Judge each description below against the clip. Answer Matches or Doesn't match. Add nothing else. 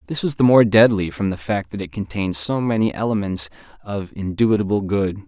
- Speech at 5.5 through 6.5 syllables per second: Matches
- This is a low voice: Matches